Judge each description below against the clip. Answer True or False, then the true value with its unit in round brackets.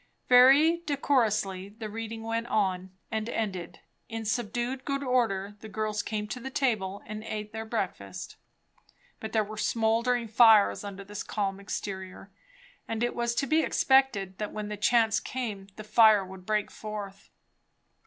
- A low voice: False (215 Hz)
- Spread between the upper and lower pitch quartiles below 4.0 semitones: True (2.8 semitones)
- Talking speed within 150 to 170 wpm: True (155 wpm)